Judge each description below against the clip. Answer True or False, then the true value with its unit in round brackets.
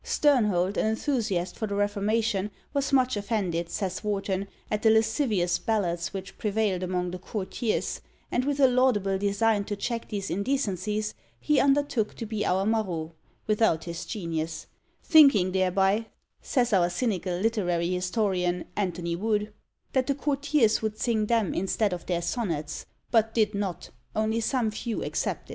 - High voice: True (210 Hz)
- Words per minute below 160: True (150 wpm)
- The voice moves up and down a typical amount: True (3.6 semitones)